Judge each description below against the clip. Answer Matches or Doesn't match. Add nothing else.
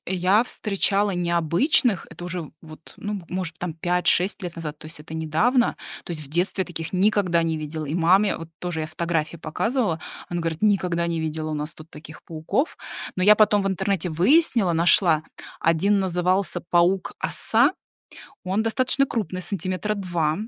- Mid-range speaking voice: Matches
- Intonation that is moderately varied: Matches